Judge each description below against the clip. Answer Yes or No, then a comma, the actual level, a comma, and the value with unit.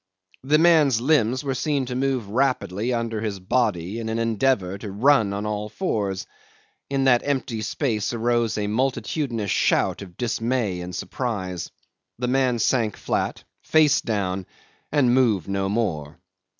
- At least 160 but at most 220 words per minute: No, average, 150 wpm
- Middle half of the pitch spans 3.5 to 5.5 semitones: Yes, average, 4.4 semitones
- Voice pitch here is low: Yes, low, 115 Hz